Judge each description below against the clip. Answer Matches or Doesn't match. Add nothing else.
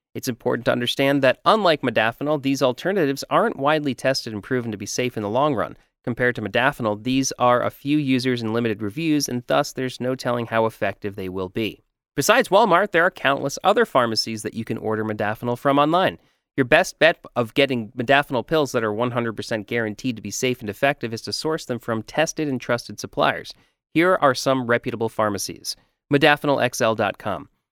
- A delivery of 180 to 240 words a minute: Matches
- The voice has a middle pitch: Doesn't match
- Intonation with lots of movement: Doesn't match